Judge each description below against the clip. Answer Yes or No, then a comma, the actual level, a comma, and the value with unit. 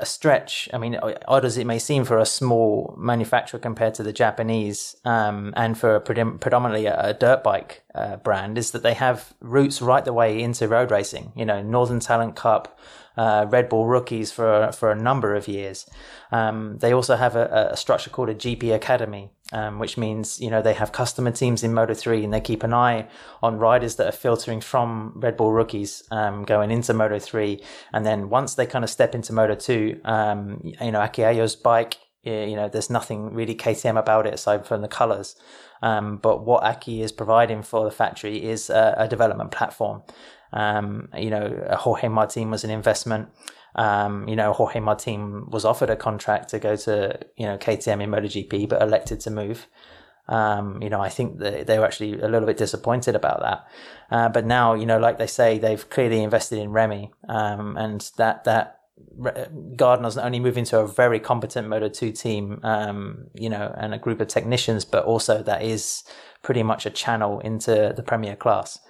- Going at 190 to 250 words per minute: Yes, average, 200 wpm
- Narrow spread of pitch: Yes, narrow, 1.6 semitones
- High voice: No, low, 110 Hz